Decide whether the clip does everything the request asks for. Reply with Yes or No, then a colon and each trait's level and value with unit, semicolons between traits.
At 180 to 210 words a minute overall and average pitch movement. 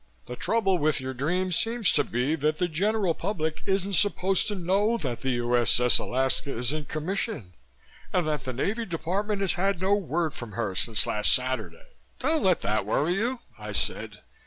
No: average, 185 wpm; wide, 7.2 semitones